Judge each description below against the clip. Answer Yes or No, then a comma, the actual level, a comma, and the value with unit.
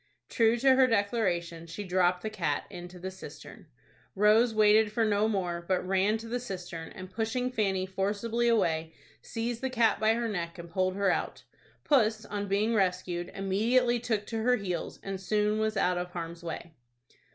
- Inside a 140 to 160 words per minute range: No, average, 180 wpm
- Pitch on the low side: No, high, 205 Hz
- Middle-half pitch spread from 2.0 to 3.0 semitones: No, average, 3.8 semitones